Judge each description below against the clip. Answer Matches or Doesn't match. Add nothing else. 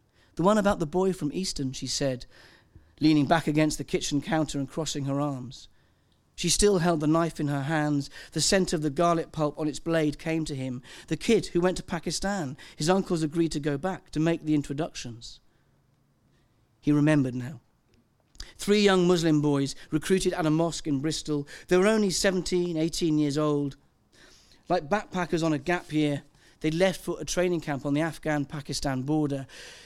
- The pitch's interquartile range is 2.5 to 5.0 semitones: Matches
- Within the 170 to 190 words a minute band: Matches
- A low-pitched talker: Doesn't match